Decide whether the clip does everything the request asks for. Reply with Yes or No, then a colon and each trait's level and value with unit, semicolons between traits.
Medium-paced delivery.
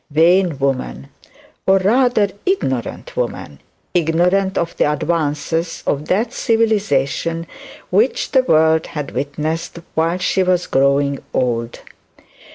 No: slow, 110 wpm